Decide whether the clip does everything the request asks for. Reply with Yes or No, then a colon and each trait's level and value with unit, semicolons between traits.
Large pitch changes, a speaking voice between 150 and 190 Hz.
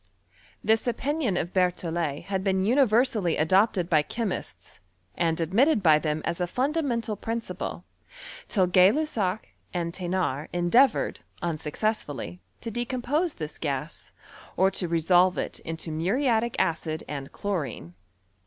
Yes: wide, 5.8 semitones; medium, 185 Hz